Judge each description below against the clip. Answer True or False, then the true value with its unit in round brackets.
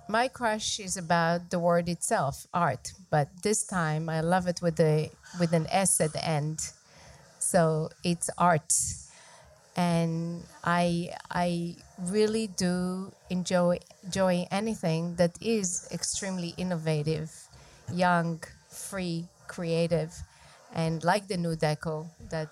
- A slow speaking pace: True (125 wpm)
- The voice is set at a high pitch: False (175 Hz)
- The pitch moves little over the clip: True (1.9 semitones)